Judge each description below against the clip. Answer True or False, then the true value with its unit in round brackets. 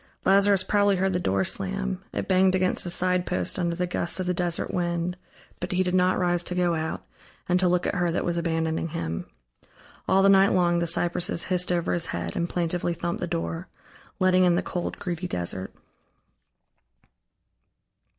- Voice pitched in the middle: True (175 Hz)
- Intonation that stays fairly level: True (1.4 semitones)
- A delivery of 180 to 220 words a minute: True (190 wpm)